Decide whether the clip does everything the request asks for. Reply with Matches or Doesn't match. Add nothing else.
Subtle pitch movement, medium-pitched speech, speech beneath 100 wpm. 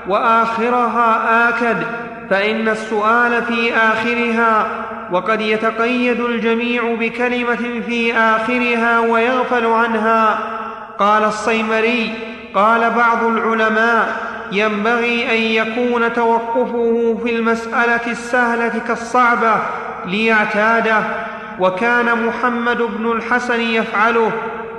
Doesn't match